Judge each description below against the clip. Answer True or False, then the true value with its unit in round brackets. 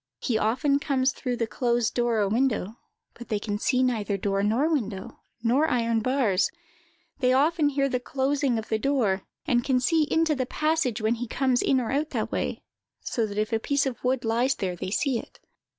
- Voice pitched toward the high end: True (245 Hz)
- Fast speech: True (210 wpm)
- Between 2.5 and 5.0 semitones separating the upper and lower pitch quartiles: True (3.8 semitones)